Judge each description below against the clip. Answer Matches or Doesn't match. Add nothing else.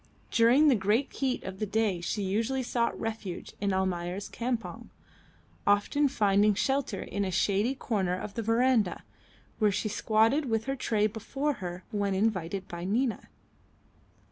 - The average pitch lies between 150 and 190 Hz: Doesn't match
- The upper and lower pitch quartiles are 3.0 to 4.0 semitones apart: Matches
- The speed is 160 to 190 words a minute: Doesn't match